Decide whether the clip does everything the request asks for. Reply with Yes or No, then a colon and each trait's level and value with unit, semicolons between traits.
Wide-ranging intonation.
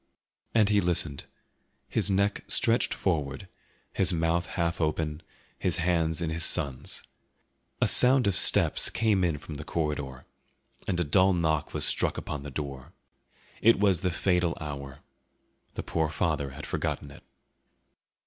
No: average, 3.8 semitones